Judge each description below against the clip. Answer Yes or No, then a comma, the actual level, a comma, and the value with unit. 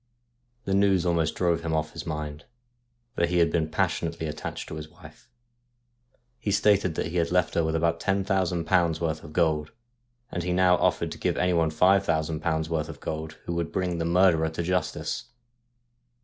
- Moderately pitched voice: No, very low, 85 Hz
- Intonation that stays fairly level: Yes, narrow, 2.2 semitones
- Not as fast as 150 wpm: No, average, 195 wpm